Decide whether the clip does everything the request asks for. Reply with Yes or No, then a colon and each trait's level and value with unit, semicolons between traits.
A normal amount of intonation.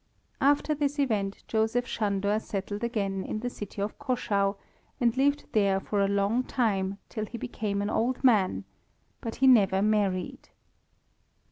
Yes: average, 3.6 semitones